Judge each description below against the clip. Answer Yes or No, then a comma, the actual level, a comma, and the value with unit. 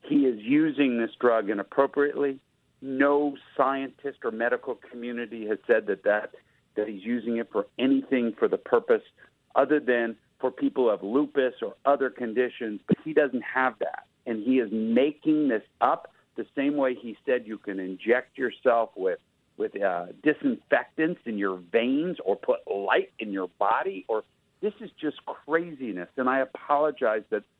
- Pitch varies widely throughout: No, average, 4.2 semitones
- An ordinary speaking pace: Yes, average, 165 wpm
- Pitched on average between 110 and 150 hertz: Yes, low, 135 Hz